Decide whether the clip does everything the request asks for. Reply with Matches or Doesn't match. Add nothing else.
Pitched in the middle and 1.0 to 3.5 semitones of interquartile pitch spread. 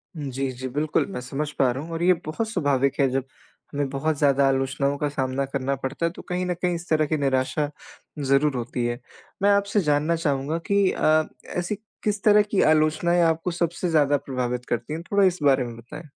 Doesn't match